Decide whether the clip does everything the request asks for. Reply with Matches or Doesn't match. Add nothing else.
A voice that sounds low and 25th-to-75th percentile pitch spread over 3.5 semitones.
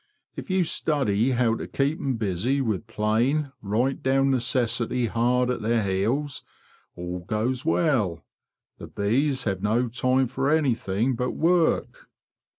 Matches